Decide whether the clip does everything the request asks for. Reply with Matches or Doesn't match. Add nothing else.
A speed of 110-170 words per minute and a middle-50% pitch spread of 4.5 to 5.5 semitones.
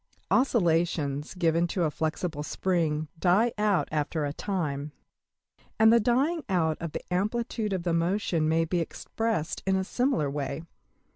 Matches